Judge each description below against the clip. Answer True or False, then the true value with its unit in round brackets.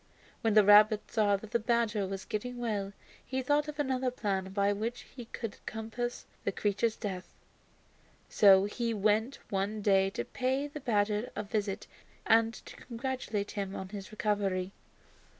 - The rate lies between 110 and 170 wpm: True (160 wpm)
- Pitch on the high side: True (215 Hz)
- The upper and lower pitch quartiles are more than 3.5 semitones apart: False (3.0 semitones)